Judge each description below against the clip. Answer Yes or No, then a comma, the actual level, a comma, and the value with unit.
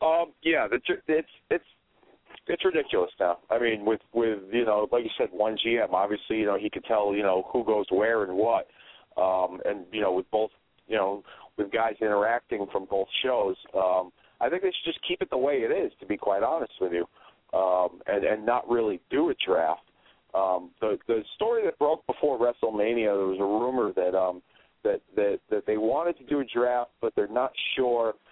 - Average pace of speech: No, fast, 210 wpm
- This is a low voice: Yes, low, 120 Hz